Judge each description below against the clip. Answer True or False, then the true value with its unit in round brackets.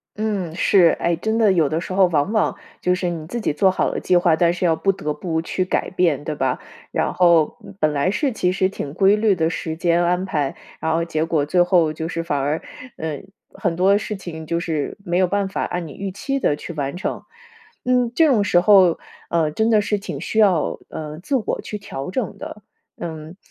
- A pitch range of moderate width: True (3.6 semitones)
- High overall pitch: False (175 Hz)